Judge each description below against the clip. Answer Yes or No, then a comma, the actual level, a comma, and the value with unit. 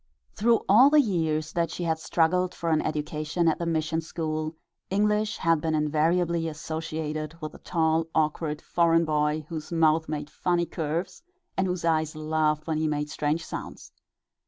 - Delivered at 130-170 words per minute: Yes, average, 165 wpm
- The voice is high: No, medium, 160 Hz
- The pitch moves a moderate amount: No, narrow, 1.7 semitones